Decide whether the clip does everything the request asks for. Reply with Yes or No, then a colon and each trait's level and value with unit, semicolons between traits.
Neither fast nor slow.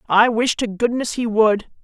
Yes: average, 195 wpm